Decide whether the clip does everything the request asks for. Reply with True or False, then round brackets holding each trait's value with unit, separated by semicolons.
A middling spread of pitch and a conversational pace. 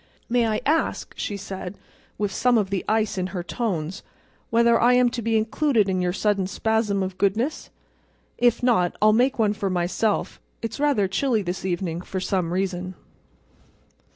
True (3.9 semitones; 170 wpm)